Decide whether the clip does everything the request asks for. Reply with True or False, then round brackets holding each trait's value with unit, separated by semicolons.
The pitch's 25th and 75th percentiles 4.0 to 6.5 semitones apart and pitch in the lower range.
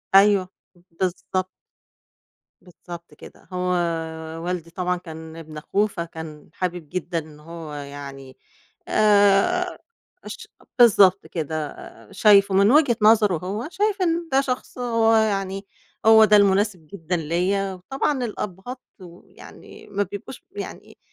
False (4.3 semitones; 190 Hz)